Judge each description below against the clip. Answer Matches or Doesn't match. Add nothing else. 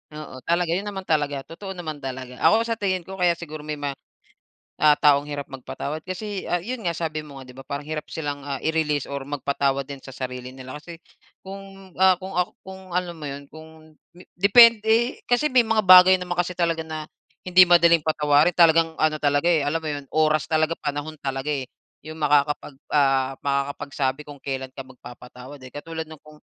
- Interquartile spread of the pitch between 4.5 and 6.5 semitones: Doesn't match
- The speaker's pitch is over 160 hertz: Doesn't match